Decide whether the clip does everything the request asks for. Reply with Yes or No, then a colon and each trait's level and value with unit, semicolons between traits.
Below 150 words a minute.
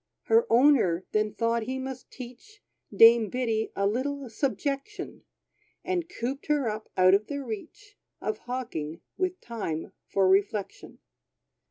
Yes: slow, 135 wpm